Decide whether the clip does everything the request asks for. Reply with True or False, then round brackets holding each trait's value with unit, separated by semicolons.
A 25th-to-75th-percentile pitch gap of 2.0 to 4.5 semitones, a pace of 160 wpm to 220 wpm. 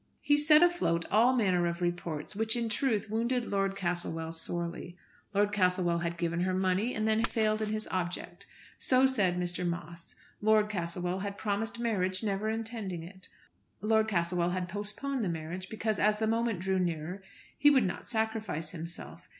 True (4.0 semitones; 175 wpm)